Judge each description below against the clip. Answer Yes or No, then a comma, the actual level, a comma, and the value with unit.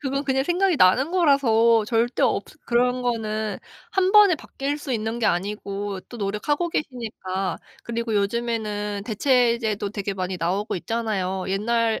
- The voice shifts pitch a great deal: No, average, 4.2 semitones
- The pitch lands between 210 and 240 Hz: Yes, high, 230 Hz